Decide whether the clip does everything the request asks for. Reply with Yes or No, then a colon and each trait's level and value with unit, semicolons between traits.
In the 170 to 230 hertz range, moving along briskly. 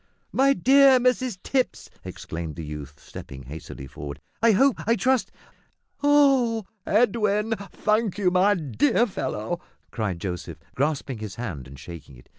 No: medium, 185 Hz; average, 145 wpm